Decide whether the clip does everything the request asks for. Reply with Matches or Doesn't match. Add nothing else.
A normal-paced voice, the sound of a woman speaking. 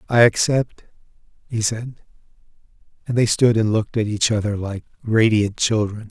Doesn't match